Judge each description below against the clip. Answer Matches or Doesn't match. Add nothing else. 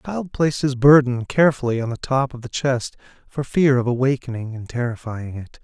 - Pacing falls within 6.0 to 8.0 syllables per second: Doesn't match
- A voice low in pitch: Matches